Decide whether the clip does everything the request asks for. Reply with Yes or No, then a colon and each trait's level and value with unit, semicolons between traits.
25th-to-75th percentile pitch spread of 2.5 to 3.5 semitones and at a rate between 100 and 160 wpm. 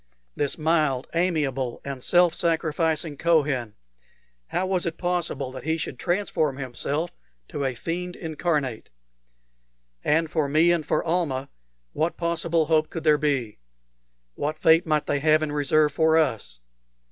Yes: average, 3.0 semitones; average, 145 wpm